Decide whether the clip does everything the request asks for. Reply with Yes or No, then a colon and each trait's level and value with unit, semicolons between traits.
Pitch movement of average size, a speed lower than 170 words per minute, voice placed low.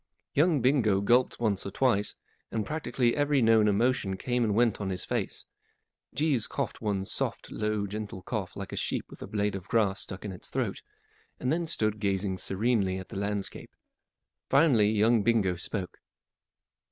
No: average, 3.7 semitones; average, 175 wpm; low, 105 Hz